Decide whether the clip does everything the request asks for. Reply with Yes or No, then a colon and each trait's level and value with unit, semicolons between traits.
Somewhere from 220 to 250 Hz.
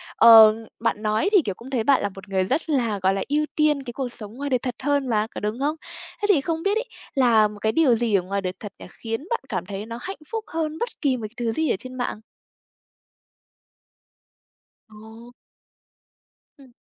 Yes: high, 240 Hz